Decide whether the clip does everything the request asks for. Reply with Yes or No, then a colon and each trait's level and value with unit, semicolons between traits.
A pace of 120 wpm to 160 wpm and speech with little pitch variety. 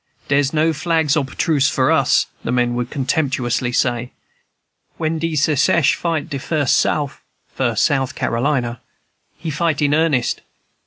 No: average, 145 wpm; average, 3.8 semitones